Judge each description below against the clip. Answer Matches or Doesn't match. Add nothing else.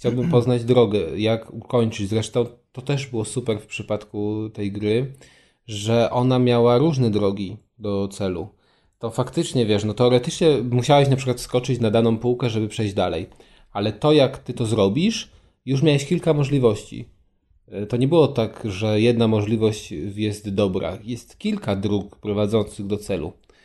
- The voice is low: Matches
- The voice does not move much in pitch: Doesn't match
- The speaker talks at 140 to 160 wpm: Matches